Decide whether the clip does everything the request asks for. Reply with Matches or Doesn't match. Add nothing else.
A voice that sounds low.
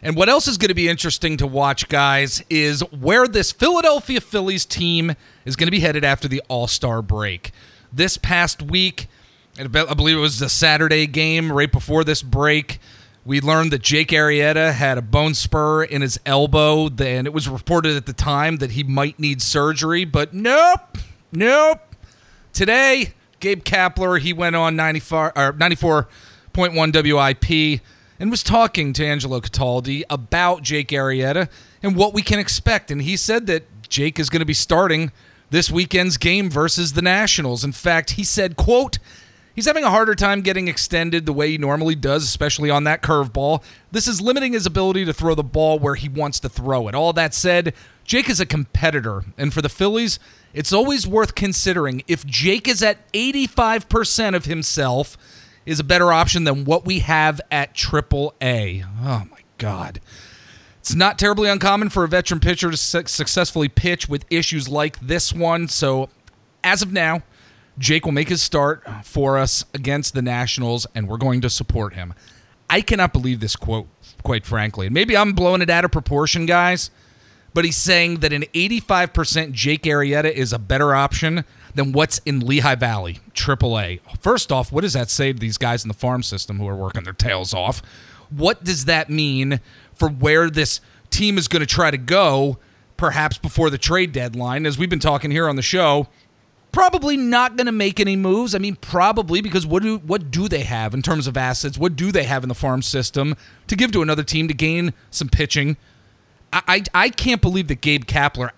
Doesn't match